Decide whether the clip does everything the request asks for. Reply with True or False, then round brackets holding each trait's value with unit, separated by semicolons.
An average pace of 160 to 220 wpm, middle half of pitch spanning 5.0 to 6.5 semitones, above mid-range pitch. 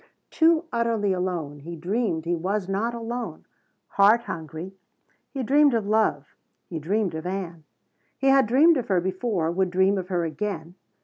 True (165 wpm; 5.3 semitones; 195 Hz)